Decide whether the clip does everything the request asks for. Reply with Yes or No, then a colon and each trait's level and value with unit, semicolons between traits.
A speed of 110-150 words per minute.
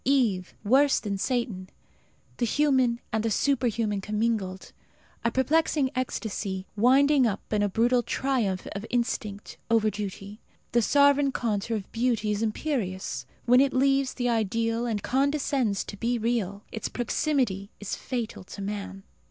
Yes: average, 145 wpm